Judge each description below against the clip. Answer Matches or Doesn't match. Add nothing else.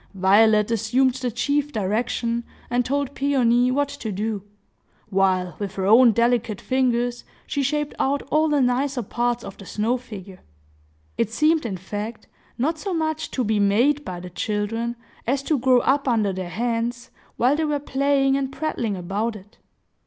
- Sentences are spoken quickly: Doesn't match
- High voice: Matches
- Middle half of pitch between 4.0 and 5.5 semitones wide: Matches